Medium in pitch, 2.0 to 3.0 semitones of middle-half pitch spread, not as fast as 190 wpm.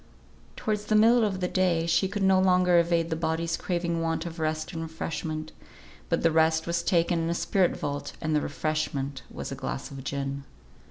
No: medium, 165 Hz; narrow, 2.5 semitones; average, 200 wpm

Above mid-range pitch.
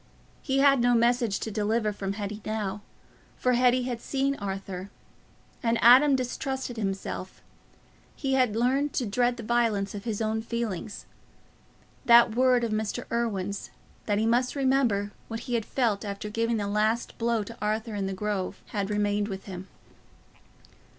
Yes: high, 225 Hz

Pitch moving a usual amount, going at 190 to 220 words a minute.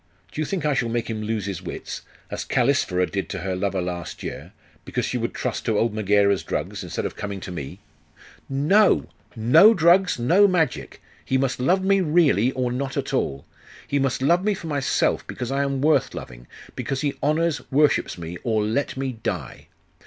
No: wide, 6.8 semitones; average, 195 wpm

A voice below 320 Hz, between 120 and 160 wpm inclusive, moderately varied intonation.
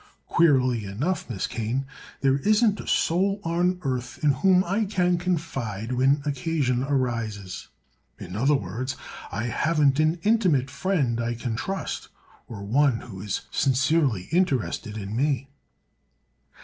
No: low, 135 Hz; slow, 135 wpm; wide, 6.0 semitones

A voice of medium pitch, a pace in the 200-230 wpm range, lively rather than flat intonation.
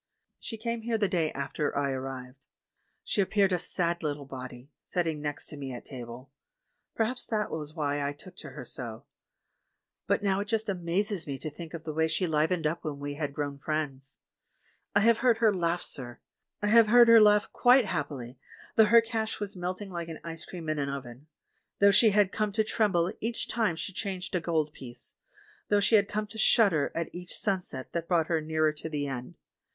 Yes: medium, 170 Hz; fast, 205 wpm; wide, 6.2 semitones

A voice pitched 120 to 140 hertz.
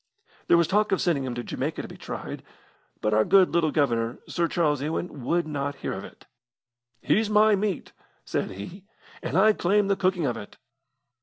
No: medium, 170 Hz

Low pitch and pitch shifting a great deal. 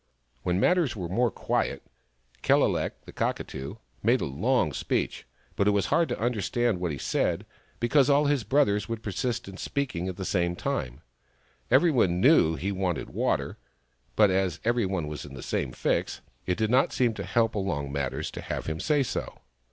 Yes: low, 100 Hz; wide, 5.9 semitones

